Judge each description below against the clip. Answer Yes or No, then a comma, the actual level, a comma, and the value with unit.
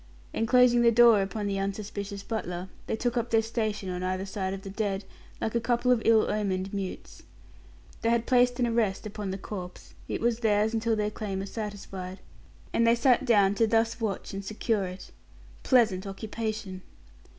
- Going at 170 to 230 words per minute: Yes, average, 185 wpm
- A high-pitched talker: Yes, high, 215 Hz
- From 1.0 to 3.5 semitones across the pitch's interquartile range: Yes, average, 2.9 semitones